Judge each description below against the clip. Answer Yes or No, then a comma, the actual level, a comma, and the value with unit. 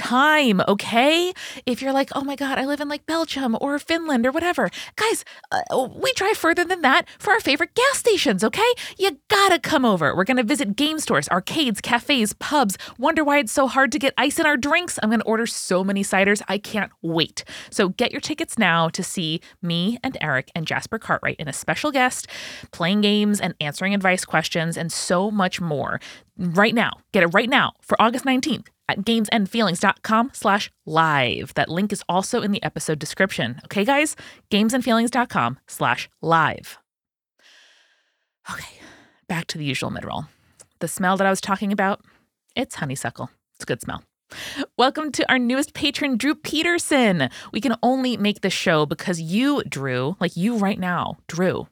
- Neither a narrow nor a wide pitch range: No, wide, 7.2 semitones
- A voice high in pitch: Yes, high, 225 Hz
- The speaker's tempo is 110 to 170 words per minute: No, average, 180 wpm